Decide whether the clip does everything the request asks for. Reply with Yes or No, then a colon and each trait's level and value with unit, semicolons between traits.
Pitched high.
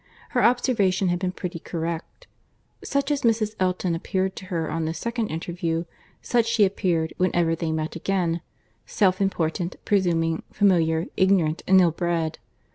No: medium, 180 Hz